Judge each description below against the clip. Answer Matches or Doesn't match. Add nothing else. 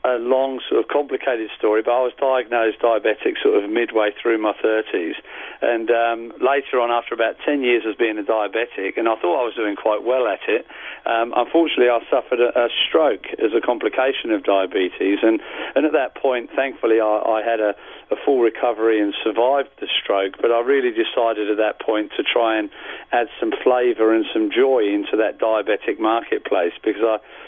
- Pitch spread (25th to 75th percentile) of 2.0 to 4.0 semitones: Matches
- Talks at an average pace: Matches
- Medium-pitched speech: Doesn't match